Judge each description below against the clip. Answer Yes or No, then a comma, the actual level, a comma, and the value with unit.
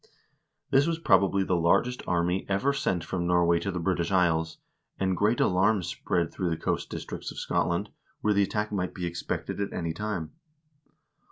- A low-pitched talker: Yes, very low, 95 Hz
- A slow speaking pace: No, average, 175 wpm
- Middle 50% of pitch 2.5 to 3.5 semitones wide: Yes, average, 3.0 semitones